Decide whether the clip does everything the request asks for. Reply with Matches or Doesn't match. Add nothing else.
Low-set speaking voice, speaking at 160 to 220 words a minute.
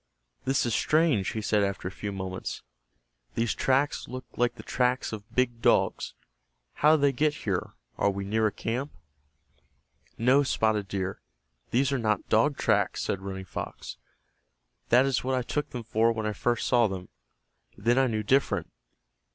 Matches